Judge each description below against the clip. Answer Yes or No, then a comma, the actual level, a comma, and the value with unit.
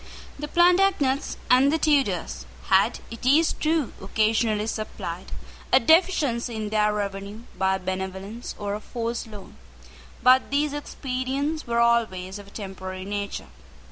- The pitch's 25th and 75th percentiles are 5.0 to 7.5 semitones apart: Yes, wide, 5.6 semitones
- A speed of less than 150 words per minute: Yes, average, 140 wpm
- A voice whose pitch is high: Yes, high, 230 Hz